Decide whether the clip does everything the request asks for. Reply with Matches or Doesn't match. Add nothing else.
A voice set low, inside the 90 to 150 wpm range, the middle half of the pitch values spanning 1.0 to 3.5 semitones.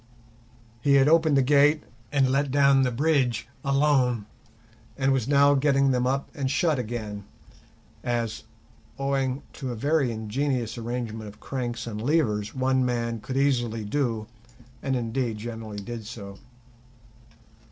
Matches